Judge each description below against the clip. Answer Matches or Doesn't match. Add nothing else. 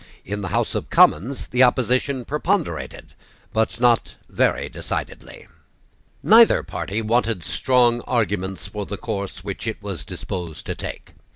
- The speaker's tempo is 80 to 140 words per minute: Matches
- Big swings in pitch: Doesn't match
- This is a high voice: Doesn't match